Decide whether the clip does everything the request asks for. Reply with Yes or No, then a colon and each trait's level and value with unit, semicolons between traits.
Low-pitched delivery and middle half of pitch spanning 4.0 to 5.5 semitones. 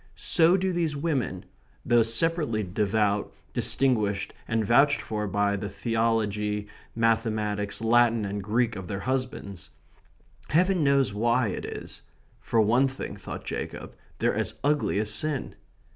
Yes: low, 115 Hz; average, 4.4 semitones